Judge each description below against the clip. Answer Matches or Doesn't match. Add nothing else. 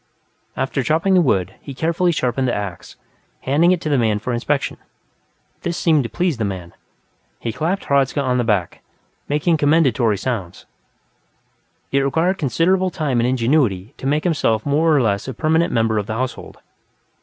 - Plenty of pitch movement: Matches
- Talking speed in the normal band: Matches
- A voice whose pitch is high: Doesn't match